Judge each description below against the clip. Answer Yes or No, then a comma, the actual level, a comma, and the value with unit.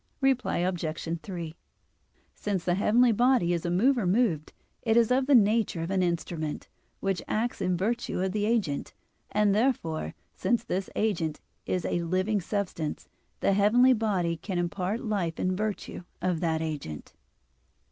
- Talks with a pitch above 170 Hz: Yes, high, 190 Hz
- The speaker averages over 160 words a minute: No, average, 155 wpm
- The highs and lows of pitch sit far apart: No, average, 4.5 semitones